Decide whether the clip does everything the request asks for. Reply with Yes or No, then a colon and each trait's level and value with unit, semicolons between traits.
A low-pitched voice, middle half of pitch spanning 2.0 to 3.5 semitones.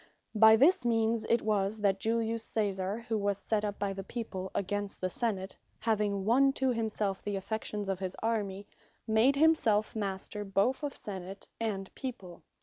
No: high, 210 Hz; narrow, 2.6 semitones